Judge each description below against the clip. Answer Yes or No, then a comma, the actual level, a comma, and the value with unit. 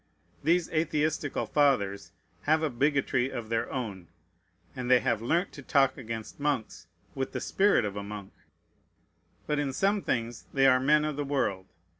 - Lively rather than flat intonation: No, average, 4.6 semitones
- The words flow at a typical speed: Yes, average, 165 wpm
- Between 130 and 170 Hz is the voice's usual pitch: Yes, low, 135 Hz